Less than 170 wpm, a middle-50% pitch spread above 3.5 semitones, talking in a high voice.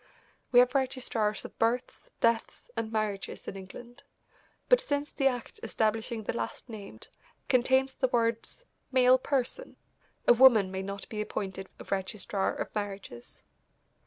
Yes: average, 140 wpm; average, 4.1 semitones; high, 230 Hz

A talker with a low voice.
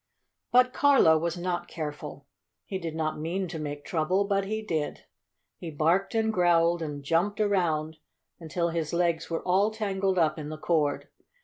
No: medium, 170 Hz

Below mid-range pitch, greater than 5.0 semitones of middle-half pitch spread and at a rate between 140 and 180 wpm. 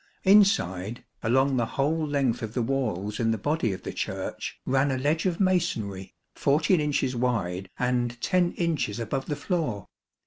Yes: low, 130 Hz; wide, 5.5 semitones; average, 165 wpm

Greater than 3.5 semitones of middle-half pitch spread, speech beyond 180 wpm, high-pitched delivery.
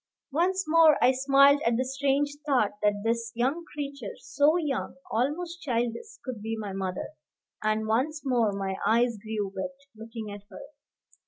No: average, 4.7 semitones; average, 160 wpm; very high, 250 Hz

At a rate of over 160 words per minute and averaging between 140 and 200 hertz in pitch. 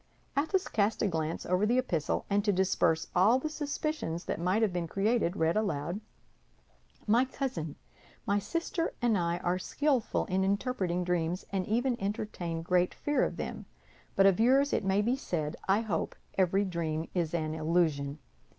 Yes: average, 170 wpm; high, 190 Hz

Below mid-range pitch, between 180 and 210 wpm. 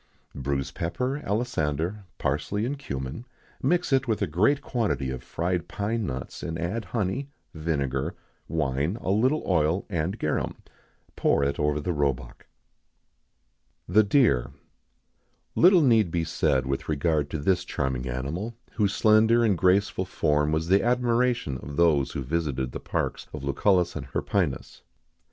No: very low, 85 Hz; average, 150 wpm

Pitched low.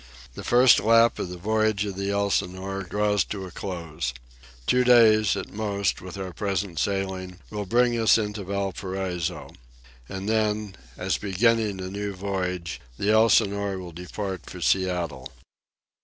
Yes: low, 100 Hz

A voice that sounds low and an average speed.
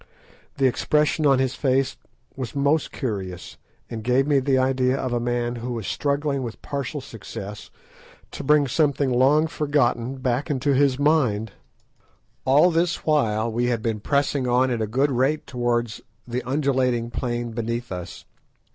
Yes: low, 130 Hz; average, 160 wpm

